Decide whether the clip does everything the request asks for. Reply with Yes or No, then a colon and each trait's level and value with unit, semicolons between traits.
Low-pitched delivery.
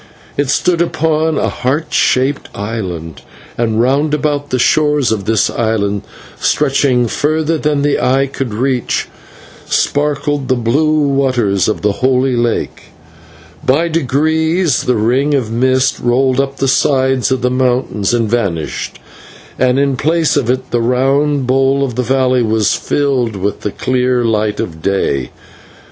Yes: low, 130 Hz